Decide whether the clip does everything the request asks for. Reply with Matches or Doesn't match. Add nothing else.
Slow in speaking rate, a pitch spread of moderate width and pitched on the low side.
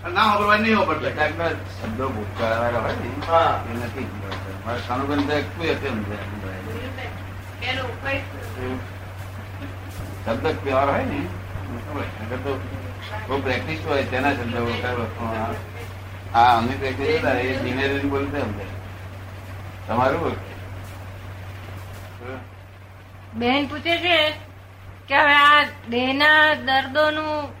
Doesn't match